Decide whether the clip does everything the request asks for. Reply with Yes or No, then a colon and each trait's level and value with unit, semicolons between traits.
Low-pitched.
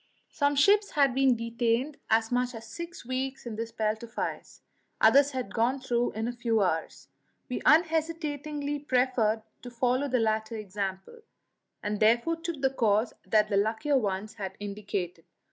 No: high, 240 Hz